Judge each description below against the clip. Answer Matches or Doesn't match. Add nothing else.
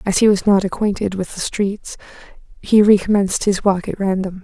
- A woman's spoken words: Matches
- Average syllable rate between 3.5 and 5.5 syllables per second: Matches